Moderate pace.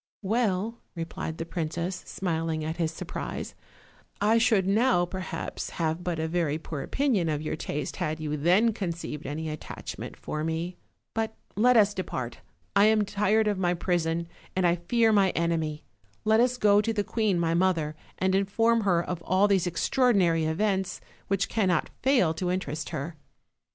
Yes: average, 170 wpm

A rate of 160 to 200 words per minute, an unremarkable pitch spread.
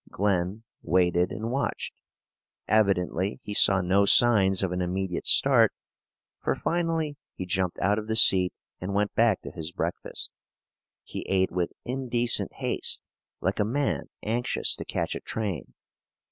No: average, 145 wpm; average, 3.9 semitones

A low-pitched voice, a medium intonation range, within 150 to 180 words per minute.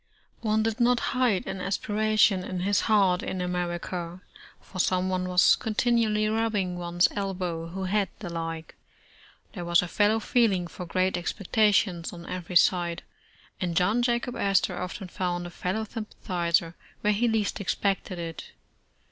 No: medium, 185 Hz; average, 3.4 semitones; average, 155 wpm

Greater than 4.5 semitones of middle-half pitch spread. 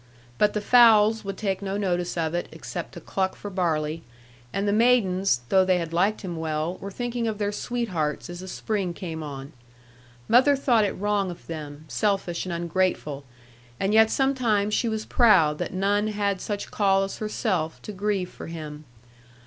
No: average, 3.8 semitones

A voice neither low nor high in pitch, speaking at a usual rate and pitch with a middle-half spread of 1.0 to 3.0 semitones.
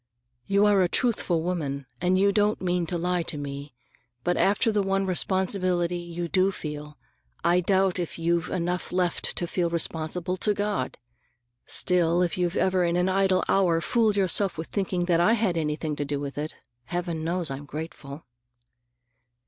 Yes: medium, 175 Hz; average, 170 wpm; narrow, 2.5 semitones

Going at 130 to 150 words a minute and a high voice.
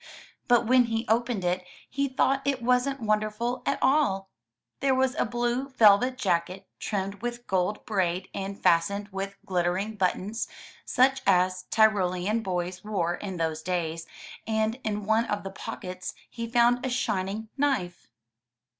Yes: average, 145 wpm; high, 210 Hz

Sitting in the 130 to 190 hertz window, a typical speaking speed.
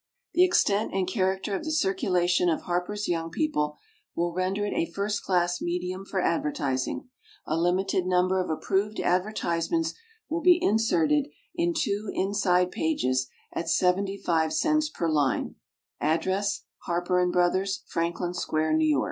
Yes: medium, 185 Hz; average, 145 wpm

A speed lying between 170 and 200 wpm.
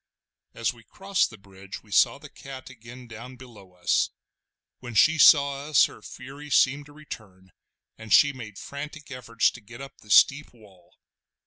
Yes: average, 175 wpm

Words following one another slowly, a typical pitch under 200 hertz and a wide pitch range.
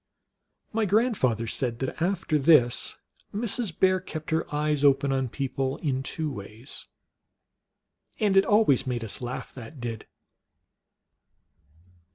Yes: slow, 125 wpm; medium, 140 Hz; wide, 6.6 semitones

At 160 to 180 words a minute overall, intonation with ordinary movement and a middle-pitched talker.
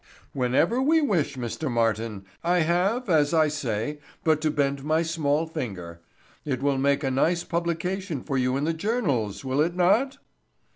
Yes: average, 165 wpm; average, 4.6 semitones; medium, 150 Hz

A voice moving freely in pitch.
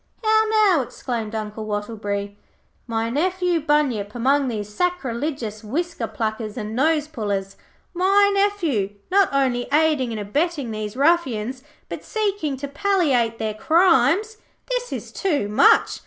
Yes: wide, 8.1 semitones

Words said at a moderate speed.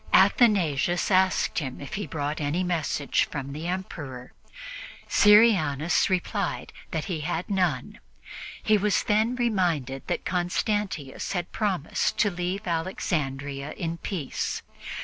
No: slow, 120 wpm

